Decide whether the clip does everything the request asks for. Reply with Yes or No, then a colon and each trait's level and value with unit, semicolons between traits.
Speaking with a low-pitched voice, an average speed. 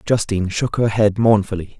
Yes: low, 105 Hz; average, 165 wpm